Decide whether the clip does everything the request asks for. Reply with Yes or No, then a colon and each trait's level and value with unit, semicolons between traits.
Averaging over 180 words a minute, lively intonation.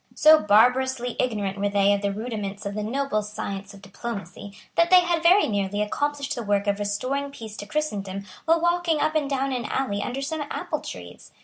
Yes: average, 200 wpm; wide, 5.7 semitones